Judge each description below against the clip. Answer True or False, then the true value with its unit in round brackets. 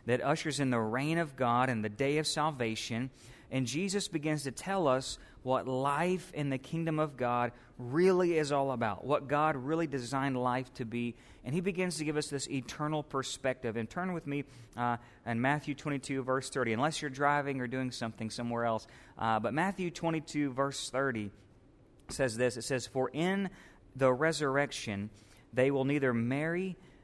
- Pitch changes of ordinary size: True (3.7 semitones)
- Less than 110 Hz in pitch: False (135 Hz)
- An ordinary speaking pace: True (180 wpm)